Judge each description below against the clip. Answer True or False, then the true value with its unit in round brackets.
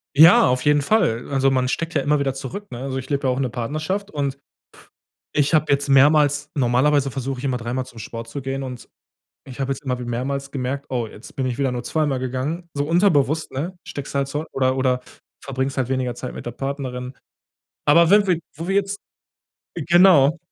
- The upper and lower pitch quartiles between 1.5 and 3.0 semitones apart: True (2.6 semitones)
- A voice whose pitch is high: False (135 Hz)